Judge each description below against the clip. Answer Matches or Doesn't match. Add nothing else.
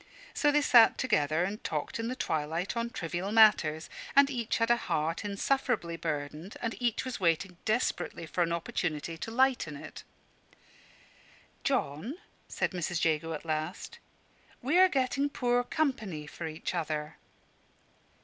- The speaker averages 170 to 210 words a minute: Doesn't match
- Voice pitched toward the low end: Doesn't match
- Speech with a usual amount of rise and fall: Doesn't match